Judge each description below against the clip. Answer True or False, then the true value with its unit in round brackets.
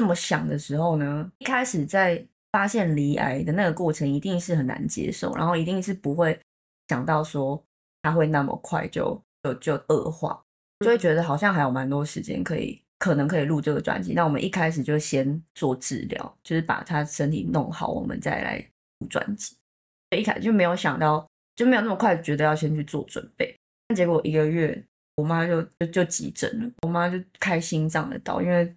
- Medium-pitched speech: True (165 Hz)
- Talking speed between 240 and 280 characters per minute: False (295 characters per minute)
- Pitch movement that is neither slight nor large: True (3.2 semitones)